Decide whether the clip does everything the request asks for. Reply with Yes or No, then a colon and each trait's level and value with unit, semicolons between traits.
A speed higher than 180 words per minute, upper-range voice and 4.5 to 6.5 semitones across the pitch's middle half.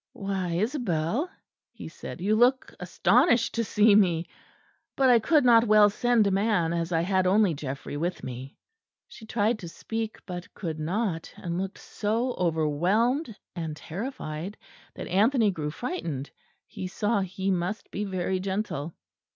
No: average, 150 wpm; high, 195 Hz; average, 4.8 semitones